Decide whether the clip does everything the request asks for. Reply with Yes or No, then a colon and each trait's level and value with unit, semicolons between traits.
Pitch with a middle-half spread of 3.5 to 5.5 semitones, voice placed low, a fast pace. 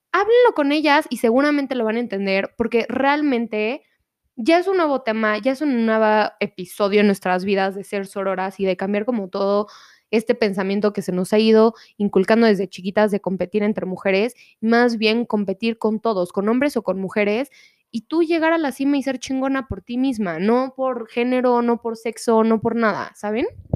No: average, 3.8 semitones; high, 225 Hz; fast, 195 wpm